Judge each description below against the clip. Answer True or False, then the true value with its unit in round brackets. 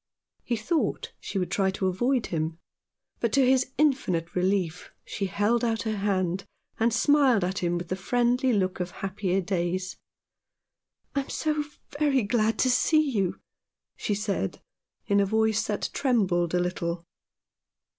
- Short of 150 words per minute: False (155 wpm)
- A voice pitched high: True (205 Hz)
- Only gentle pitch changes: False (4.9 semitones)